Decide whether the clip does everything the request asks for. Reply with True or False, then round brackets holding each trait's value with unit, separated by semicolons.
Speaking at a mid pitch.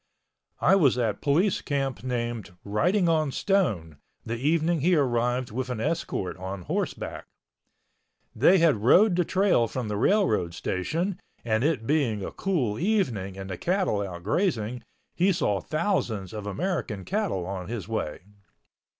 False (125 Hz)